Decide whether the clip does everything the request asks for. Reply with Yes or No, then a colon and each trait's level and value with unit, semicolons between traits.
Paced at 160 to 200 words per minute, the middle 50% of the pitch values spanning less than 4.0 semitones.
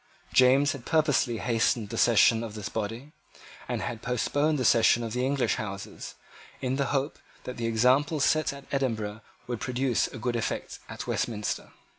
Yes: average, 170 wpm; average, 3.3 semitones